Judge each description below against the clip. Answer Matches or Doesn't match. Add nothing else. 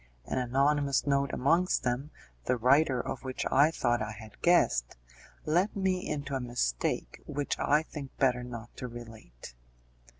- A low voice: Matches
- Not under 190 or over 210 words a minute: Doesn't match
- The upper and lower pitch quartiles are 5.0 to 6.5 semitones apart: Doesn't match